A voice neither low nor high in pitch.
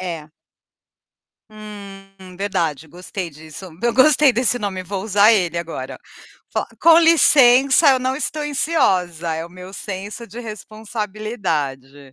No: high, 200 Hz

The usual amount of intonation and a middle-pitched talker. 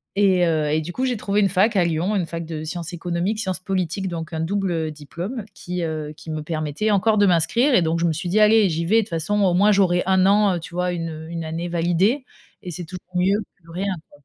Yes: average, 3.2 semitones; medium, 180 Hz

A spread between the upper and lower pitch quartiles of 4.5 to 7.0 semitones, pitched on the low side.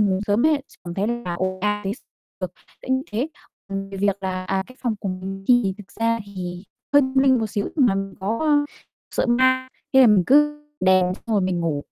No: average, 5.1 semitones; high, 205 Hz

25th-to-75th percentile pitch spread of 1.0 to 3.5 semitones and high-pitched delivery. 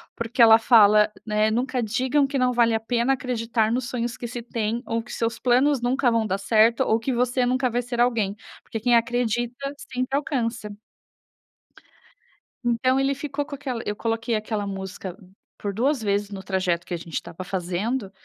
Yes: average, 2.8 semitones; high, 235 Hz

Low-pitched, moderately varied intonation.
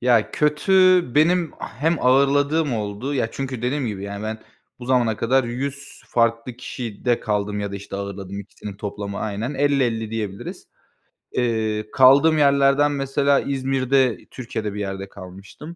Yes: low, 120 Hz; average, 4.9 semitones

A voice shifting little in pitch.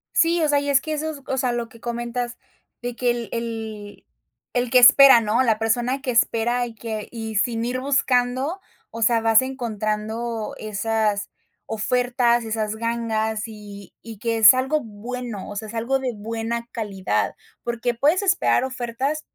Yes: narrow, 2.3 semitones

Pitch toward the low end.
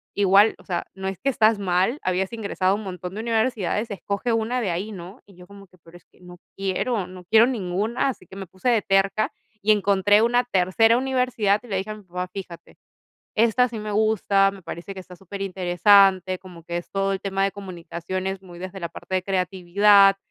No: high, 195 Hz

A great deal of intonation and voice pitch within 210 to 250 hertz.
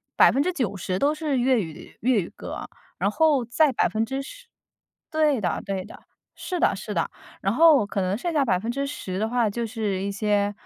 Yes: wide, 5.8 semitones; high, 235 Hz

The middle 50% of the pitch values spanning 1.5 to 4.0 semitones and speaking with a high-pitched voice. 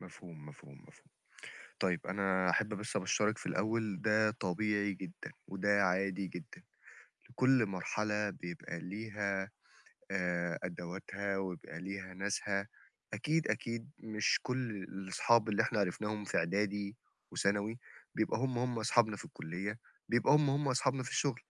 No: average, 2.9 semitones; low, 100 Hz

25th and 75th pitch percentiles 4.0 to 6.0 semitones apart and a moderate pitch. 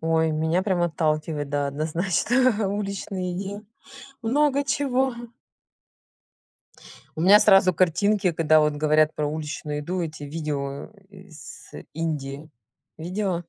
Yes: average, 4.5 semitones; medium, 165 Hz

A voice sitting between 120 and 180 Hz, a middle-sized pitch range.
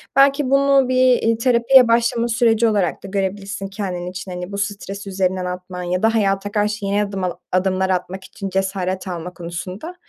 No: high, 195 Hz; average, 3.5 semitones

